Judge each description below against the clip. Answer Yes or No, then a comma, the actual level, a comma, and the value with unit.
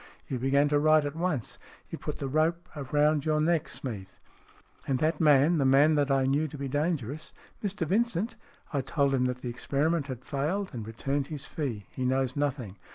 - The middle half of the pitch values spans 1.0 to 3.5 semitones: Yes, average, 2.9 semitones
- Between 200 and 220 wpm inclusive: Yes, fast, 205 wpm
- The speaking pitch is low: No, medium, 145 Hz